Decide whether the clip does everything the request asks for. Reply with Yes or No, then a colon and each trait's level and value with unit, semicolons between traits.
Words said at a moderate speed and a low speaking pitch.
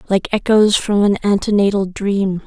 No: average, 145 wpm; high, 200 Hz